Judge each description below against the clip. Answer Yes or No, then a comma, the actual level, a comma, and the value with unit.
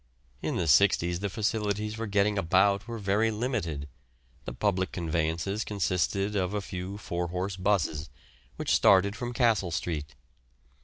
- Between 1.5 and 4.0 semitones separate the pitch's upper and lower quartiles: Yes, average, 3.2 semitones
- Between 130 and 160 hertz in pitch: No, low, 100 Hz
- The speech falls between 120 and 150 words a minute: Yes, average, 145 wpm